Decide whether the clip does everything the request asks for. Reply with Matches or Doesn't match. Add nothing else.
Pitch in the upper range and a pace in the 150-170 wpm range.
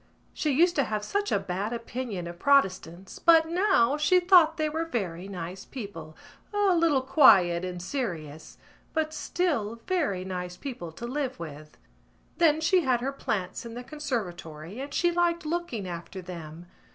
Matches